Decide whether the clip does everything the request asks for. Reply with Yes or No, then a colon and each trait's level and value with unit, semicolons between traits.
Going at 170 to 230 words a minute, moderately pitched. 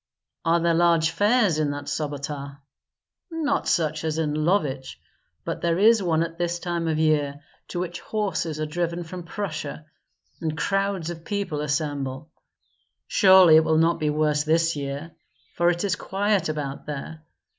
No: average, 160 wpm; medium, 165 Hz